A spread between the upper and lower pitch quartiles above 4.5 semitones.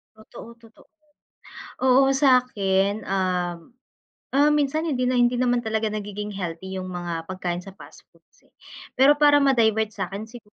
Yes: average, 4.9 semitones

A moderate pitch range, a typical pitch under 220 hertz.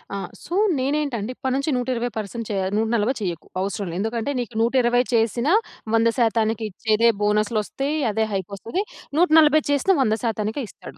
No: average, 3.6 semitones; high, 230 Hz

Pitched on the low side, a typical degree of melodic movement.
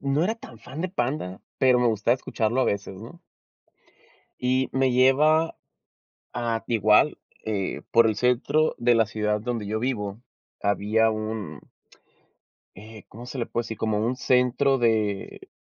Yes: low, 115 Hz; average, 3.2 semitones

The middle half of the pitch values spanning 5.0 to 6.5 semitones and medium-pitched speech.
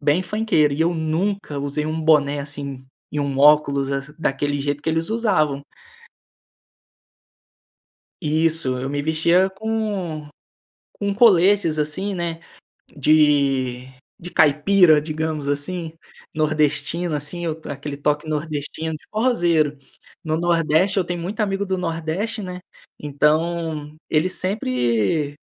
No: average, 3.4 semitones; medium, 155 Hz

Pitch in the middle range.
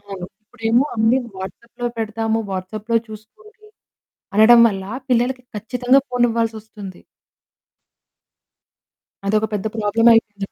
No: high, 225 Hz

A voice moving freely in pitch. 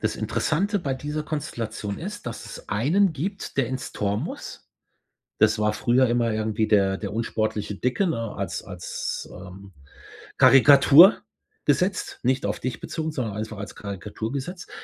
Yes: wide, 6.2 semitones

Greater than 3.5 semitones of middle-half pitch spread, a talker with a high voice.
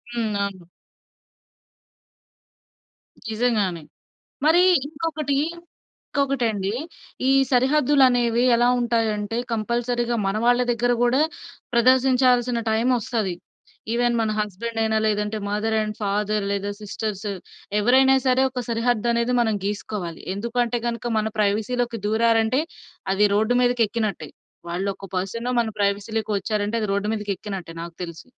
No: average, 2.8 semitones; high, 225 Hz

